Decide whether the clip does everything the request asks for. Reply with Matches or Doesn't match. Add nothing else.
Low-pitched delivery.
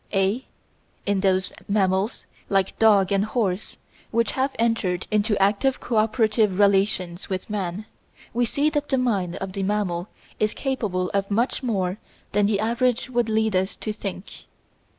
Doesn't match